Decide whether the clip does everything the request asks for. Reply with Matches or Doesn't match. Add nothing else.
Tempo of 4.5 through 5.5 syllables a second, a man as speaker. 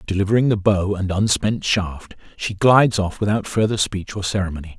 Matches